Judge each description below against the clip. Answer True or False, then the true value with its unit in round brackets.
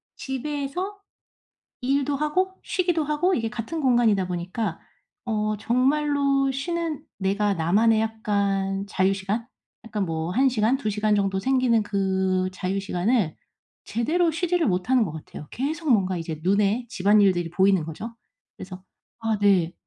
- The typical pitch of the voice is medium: False (215 Hz)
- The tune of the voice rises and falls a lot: True (6.0 semitones)